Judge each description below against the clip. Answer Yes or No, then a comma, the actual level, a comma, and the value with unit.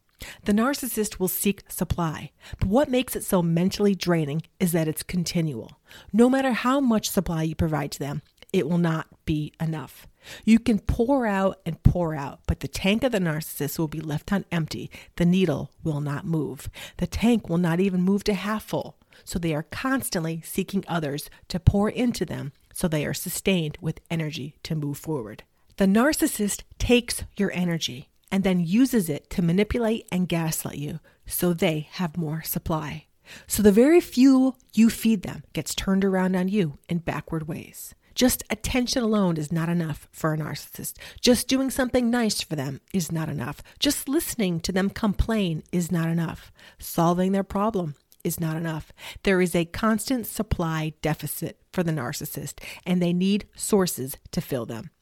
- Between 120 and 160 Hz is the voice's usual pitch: No, medium, 175 Hz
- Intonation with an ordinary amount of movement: Yes, average, 4.8 semitones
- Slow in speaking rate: No, average, 180 wpm